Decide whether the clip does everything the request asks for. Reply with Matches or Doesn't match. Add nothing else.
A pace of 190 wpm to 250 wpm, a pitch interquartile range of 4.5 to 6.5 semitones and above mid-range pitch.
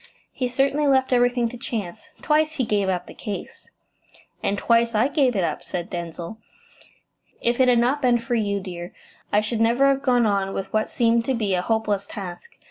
Doesn't match